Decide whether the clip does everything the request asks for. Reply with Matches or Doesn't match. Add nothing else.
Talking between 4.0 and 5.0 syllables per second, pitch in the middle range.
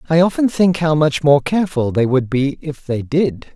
Matches